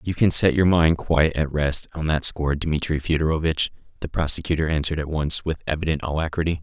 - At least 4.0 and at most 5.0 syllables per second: No, 6.1 syllables/s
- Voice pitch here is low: Yes, very low, 80 Hz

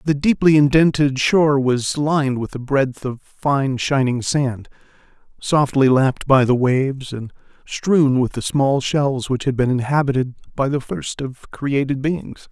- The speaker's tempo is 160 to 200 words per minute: Yes, average, 165 wpm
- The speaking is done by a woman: No, male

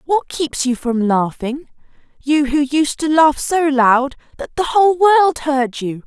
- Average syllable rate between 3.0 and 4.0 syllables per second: Yes, 3.9 syllables/s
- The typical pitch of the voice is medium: No, very high, 285 Hz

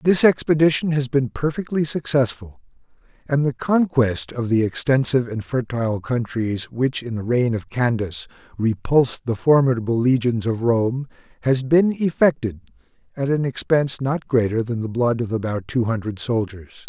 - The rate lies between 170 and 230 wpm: No, average, 155 wpm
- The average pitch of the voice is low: Yes, low, 125 Hz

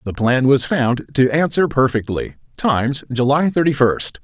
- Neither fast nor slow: Yes, average, 155 wpm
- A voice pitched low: Yes, low, 130 Hz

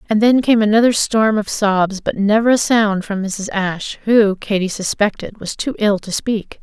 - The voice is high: Yes, high, 210 Hz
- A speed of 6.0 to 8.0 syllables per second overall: No, 4.6 syllables/s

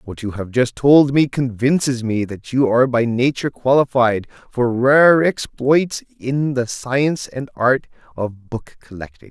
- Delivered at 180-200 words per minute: No, average, 160 wpm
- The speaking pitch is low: Yes, low, 125 Hz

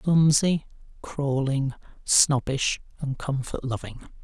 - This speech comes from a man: Yes, male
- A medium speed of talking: No, slow, 85 wpm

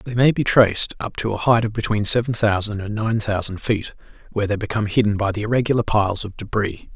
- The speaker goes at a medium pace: No, fast, 225 wpm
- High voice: No, low, 105 Hz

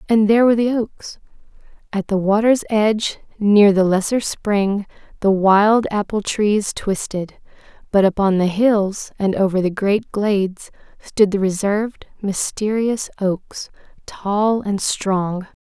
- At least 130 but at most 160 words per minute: Yes, slow, 135 wpm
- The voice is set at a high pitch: Yes, high, 205 Hz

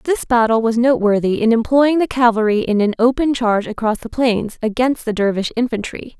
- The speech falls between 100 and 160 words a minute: No, average, 185 wpm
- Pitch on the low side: No, high, 235 Hz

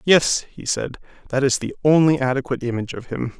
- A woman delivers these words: No, male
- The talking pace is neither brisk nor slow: Yes, average, 195 wpm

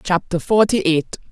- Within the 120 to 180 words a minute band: Yes, slow, 135 wpm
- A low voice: No, medium, 185 Hz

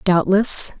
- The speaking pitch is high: Yes, high, 195 Hz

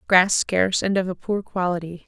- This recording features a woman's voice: Yes, female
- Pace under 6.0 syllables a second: Yes, 5.2 syllables/s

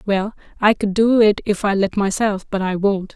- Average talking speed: No, fast, 230 wpm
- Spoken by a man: No, female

